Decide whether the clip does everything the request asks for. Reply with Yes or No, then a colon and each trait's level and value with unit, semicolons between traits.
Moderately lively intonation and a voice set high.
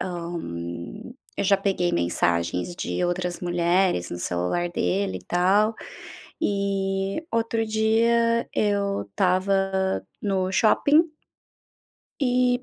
Yes: average, 3.5 semitones; high, 195 Hz